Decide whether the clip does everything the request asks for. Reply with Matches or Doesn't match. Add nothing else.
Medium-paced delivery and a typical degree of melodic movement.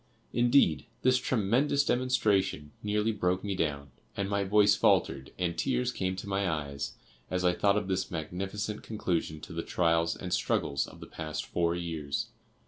Matches